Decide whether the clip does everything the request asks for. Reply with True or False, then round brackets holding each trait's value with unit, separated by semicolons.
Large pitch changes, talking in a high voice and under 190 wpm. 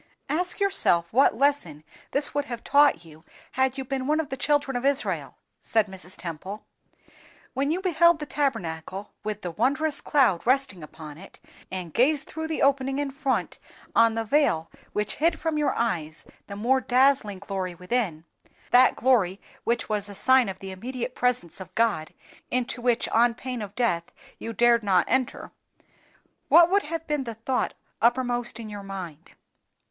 True (6.1 semitones; 240 Hz; 165 wpm)